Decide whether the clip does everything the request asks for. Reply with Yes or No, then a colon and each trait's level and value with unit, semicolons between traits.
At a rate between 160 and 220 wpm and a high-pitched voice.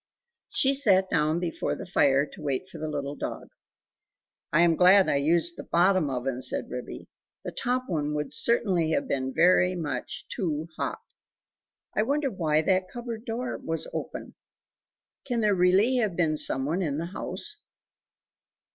No: average, 165 wpm; medium, 175 Hz